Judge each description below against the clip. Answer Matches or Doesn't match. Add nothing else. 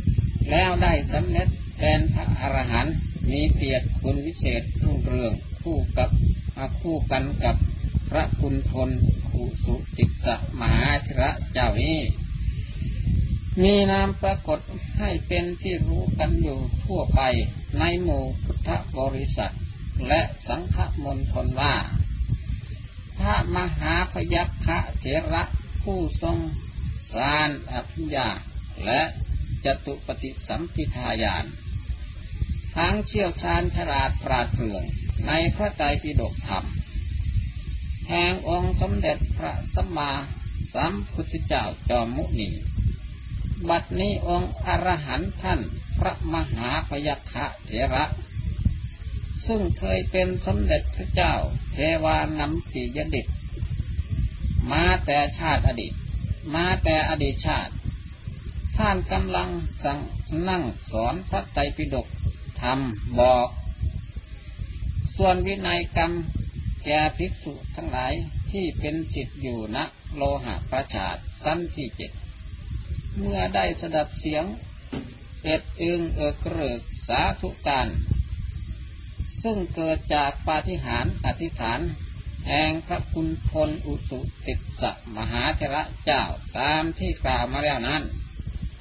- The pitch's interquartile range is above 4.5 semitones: Matches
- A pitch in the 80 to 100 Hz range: Matches